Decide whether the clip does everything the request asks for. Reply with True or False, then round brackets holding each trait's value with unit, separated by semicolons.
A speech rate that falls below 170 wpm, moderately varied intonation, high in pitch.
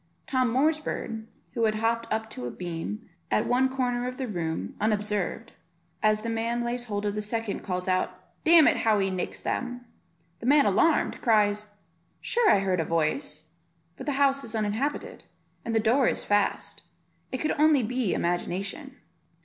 False (175 wpm; 3.9 semitones; 225 Hz)